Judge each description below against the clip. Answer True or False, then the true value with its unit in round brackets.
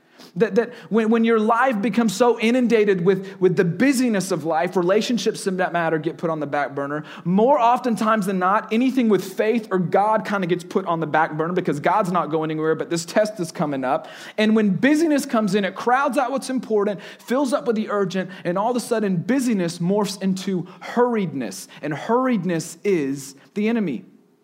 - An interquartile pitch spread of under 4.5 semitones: False (4.9 semitones)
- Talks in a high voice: True (200 Hz)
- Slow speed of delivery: False (200 wpm)